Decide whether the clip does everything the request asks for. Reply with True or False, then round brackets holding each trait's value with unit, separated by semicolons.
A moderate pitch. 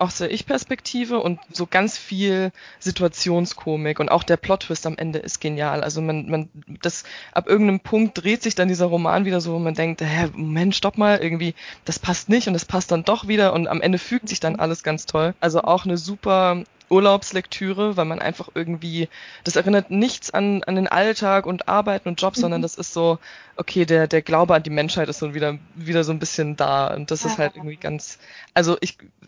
True (175 Hz)